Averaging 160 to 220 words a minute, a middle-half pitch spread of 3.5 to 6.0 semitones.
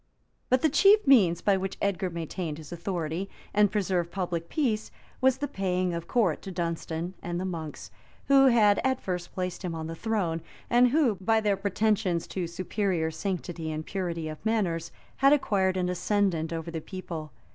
Yes: average, 180 wpm; average, 3.9 semitones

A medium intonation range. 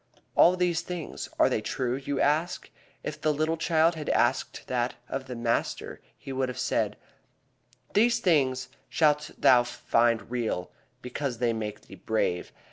Yes: average, 4.7 semitones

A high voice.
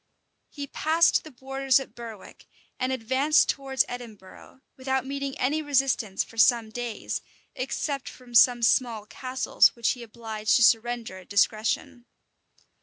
Yes: high, 245 Hz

